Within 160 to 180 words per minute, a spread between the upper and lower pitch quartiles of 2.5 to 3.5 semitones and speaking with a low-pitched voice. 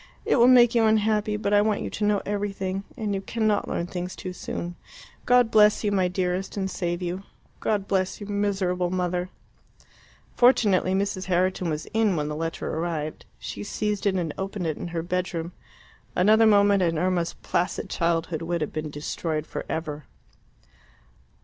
No: average, 175 wpm; average, 3.2 semitones; medium, 185 Hz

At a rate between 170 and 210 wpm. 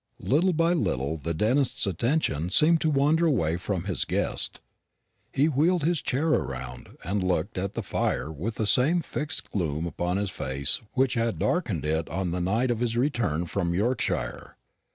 Yes: average, 175 wpm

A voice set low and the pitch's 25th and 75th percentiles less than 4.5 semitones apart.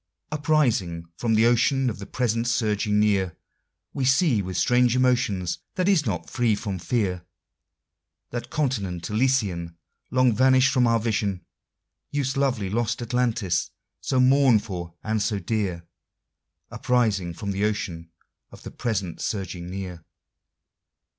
No: low, 110 Hz; average, 4.8 semitones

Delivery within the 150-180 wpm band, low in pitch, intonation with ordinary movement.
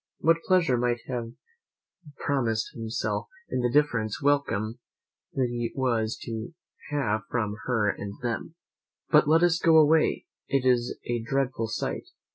No: average, 140 wpm; low, 120 Hz; average, 4.1 semitones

